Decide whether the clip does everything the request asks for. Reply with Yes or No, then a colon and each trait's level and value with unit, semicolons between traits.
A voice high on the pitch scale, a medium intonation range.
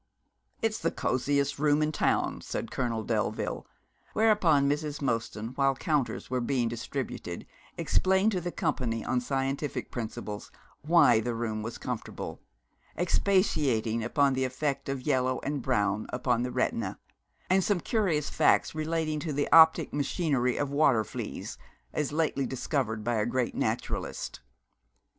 No: low, 135 Hz; average, 4.3 semitones